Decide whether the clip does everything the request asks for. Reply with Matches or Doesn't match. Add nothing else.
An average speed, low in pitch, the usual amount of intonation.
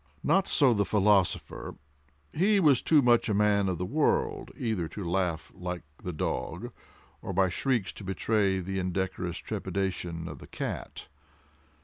Matches